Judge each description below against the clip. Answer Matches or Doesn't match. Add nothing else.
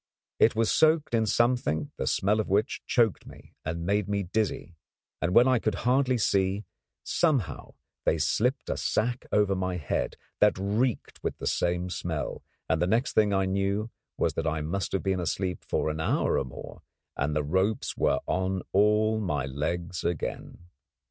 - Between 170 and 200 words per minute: Matches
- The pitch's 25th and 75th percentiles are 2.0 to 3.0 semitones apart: Doesn't match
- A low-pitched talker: Matches